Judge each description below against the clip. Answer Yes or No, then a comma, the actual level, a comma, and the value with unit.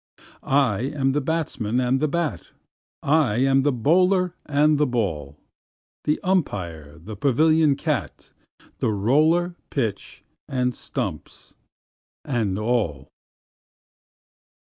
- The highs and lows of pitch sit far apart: Yes, wide, 6.0 semitones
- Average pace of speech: No, slow, 105 wpm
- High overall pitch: No, low, 135 Hz